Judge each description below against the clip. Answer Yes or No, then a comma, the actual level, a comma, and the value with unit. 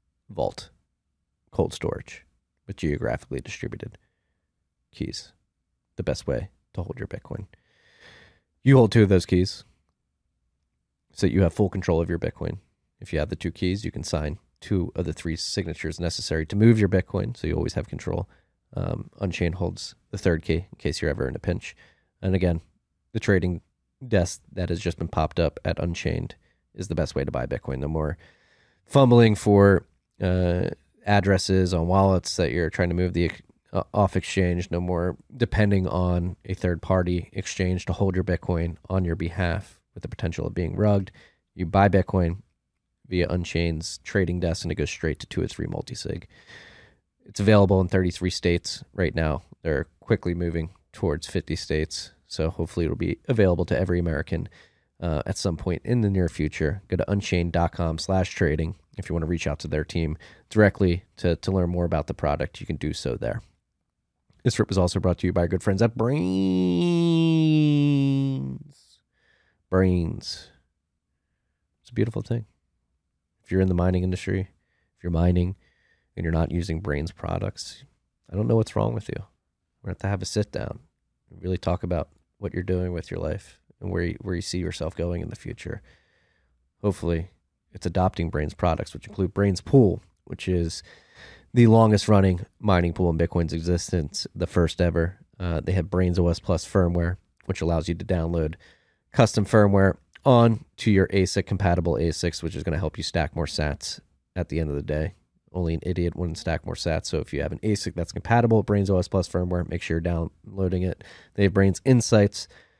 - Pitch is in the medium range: No, very low, 90 Hz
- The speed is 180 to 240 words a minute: Yes, average, 185 wpm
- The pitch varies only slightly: No, average, 3.1 semitones